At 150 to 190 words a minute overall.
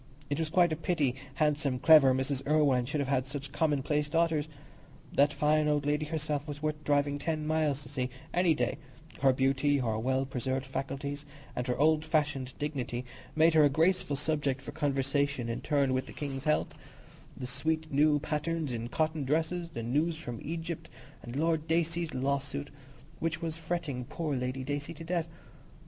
Yes: average, 175 wpm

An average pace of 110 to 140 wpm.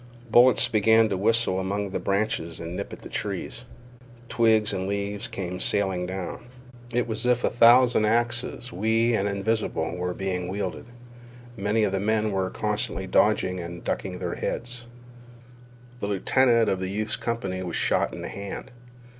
No: average, 165 wpm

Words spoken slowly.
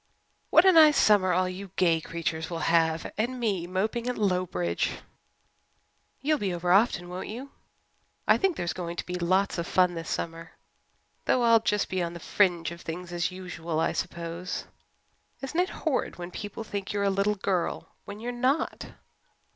No: average, 180 wpm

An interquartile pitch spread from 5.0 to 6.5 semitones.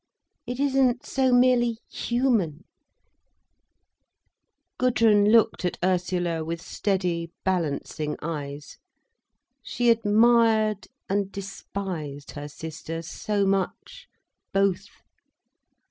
Yes: wide, 5.5 semitones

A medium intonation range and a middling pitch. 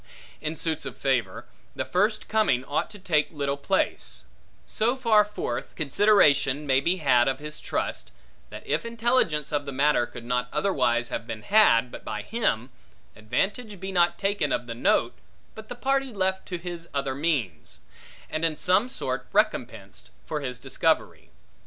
No: wide, 7.6 semitones; medium, 150 Hz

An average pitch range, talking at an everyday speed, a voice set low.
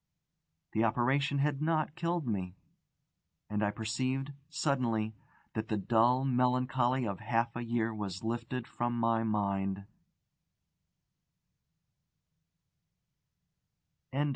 No: average, 3.2 semitones; slow, 95 wpm; low, 120 Hz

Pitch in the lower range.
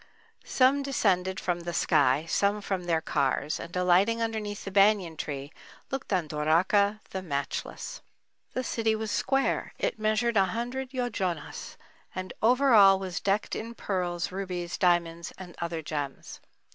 No: high, 190 Hz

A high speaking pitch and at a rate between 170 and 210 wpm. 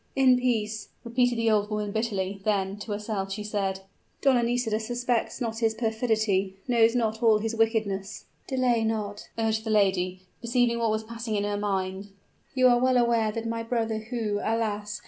Yes: high, 220 Hz; average, 175 wpm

